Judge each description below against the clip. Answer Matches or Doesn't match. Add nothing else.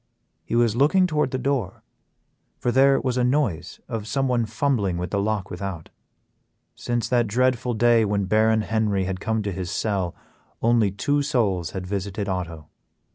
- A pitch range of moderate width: Matches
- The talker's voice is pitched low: Matches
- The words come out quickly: Doesn't match